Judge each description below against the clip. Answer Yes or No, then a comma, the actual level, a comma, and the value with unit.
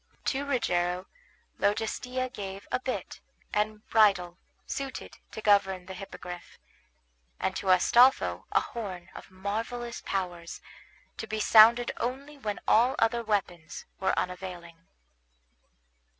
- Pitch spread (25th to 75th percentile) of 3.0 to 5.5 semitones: Yes, average, 4.5 semitones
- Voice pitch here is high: Yes, high, 205 Hz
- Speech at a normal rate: No, slow, 115 wpm